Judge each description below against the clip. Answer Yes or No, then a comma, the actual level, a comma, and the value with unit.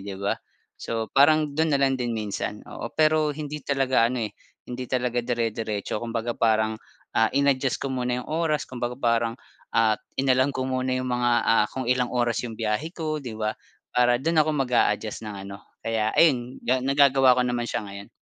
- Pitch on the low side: Yes, low, 125 Hz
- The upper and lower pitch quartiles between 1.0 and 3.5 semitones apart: Yes, average, 3.2 semitones